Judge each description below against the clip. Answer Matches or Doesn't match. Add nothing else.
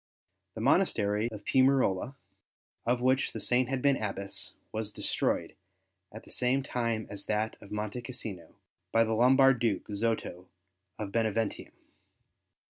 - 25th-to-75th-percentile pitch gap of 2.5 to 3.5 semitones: Matches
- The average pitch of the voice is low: Matches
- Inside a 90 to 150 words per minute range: Matches